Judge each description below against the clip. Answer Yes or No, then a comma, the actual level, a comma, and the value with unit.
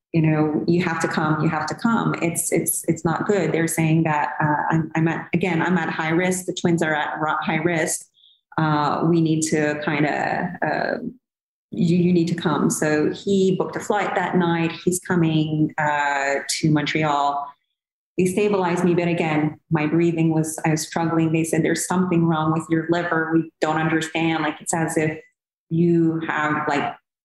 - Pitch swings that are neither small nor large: No, narrow, 1.9 semitones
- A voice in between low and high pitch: Yes, medium, 165 Hz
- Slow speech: No, average, 190 wpm